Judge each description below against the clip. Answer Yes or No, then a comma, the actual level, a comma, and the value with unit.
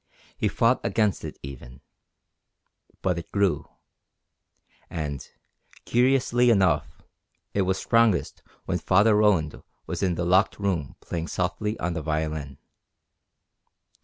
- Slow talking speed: Yes, slow, 115 wpm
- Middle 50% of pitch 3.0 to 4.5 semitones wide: No, average, 4.9 semitones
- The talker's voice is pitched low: Yes, very low, 95 Hz